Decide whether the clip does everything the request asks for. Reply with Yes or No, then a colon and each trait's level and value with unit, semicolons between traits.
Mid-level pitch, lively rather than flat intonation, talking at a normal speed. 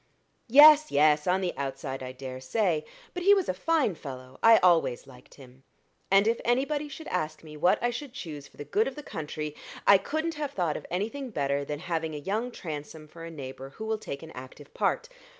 No: medium, 165 Hz; wide, 8.6 semitones; fast, 215 wpm